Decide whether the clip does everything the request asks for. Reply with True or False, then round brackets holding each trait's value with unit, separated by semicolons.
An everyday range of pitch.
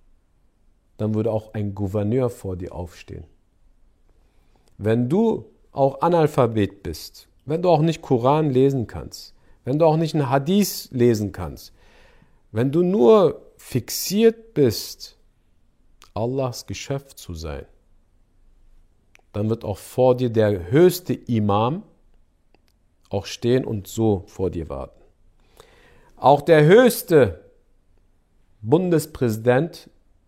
False (7.4 semitones)